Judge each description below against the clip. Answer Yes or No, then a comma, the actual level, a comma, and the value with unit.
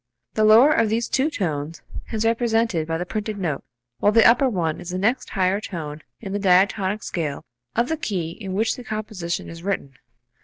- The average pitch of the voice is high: Yes, high, 200 Hz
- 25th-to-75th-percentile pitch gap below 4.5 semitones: No, average, 4.8 semitones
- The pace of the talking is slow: No, average, 195 wpm